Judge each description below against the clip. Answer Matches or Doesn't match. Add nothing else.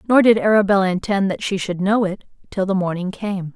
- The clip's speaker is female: Matches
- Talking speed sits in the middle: Doesn't match